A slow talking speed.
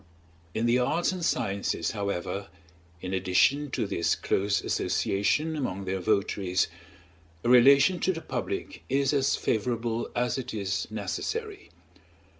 Yes: slow, 130 wpm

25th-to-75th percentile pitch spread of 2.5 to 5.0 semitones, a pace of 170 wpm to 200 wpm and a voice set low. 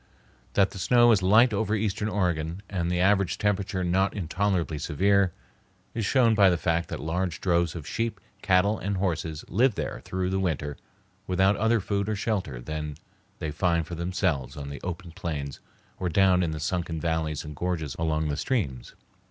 Yes: average, 3.9 semitones; average, 180 wpm; very low, 90 Hz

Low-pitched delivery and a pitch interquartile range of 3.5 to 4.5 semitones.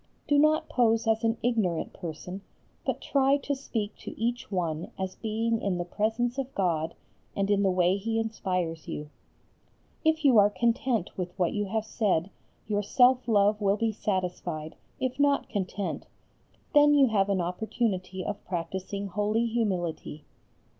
No: high, 205 Hz; average, 4.1 semitones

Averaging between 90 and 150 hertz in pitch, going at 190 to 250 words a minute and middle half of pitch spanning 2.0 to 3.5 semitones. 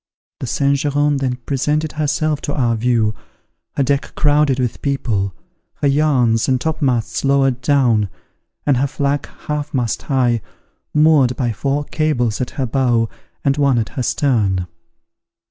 No: low, 135 Hz; average, 145 wpm; average, 3.2 semitones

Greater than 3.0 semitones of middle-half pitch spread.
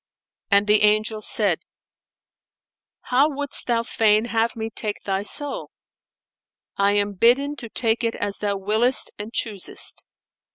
No: narrow, 2.4 semitones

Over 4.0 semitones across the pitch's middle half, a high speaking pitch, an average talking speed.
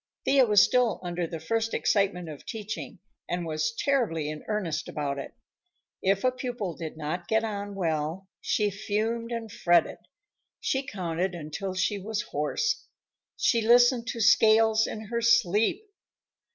Yes: average, 4.9 semitones; high, 205 Hz; average, 150 wpm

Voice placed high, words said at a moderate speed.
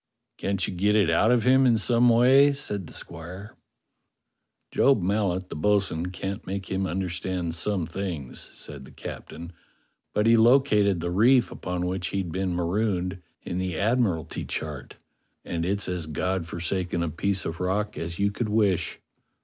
No: very low, 95 Hz; average, 165 wpm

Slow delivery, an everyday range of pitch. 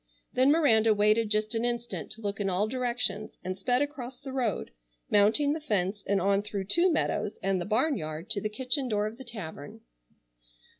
No: average, 190 wpm; average, 4.0 semitones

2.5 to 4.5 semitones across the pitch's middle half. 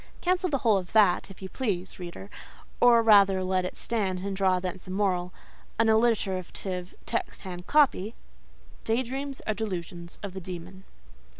Yes: average, 3.5 semitones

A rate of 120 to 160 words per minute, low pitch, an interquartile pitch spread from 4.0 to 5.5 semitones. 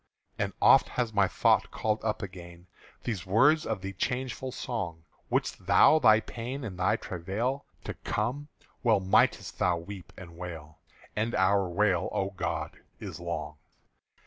Yes: average, 155 wpm; low, 100 Hz; average, 4.6 semitones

